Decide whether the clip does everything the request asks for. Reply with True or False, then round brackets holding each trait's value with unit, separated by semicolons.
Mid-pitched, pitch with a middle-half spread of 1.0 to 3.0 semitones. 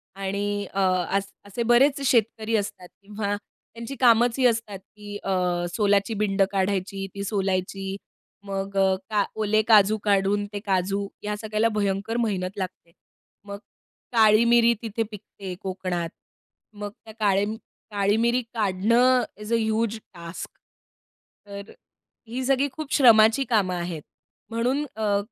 False (205 Hz; 2.5 semitones)